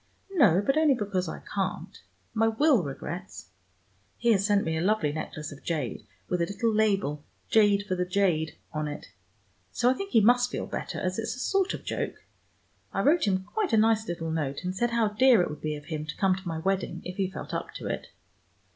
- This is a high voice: Yes, high, 195 Hz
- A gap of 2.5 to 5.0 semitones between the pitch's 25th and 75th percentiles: No, wide, 5.4 semitones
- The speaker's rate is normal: No, fast, 220 wpm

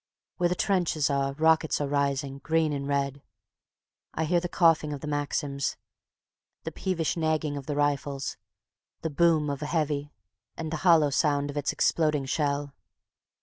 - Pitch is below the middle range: No, medium, 150 Hz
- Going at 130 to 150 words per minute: No, average, 160 wpm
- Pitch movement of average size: No, narrow, 2.1 semitones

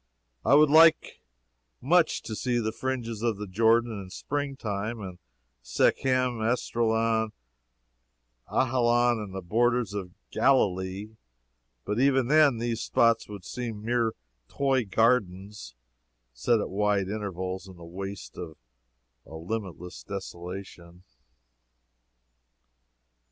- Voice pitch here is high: No, low, 110 Hz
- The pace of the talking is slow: Yes, slow, 115 wpm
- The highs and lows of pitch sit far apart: No, average, 4.1 semitones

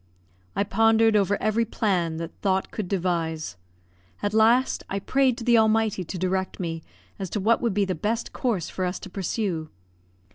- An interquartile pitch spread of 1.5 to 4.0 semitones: Yes, average, 3.6 semitones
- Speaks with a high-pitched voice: Yes, high, 200 Hz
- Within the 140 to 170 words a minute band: No, average, 180 wpm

